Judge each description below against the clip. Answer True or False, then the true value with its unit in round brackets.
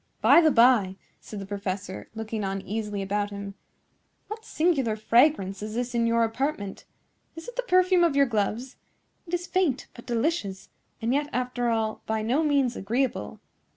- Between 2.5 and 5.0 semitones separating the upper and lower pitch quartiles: False (5.5 semitones)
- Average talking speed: True (165 wpm)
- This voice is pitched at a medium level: False (235 Hz)